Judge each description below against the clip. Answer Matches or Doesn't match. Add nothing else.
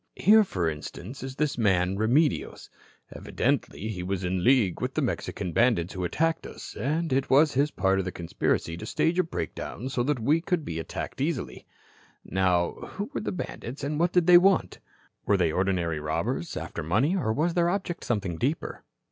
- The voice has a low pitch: Matches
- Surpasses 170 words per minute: Matches